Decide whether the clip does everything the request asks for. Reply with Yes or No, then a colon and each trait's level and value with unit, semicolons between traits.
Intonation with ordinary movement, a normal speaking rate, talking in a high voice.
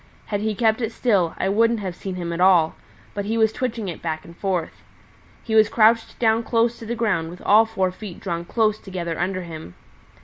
No: average, 4.1 semitones; fast, 215 wpm; high, 205 Hz